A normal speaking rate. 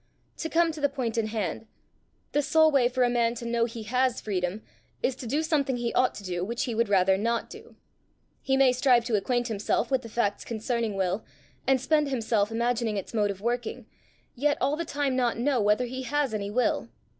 No: fast, 215 wpm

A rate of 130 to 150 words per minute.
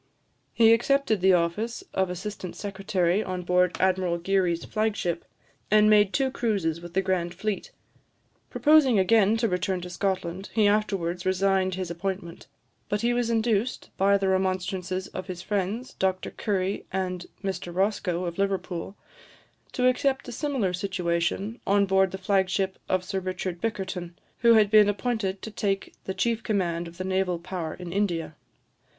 No: average, 160 wpm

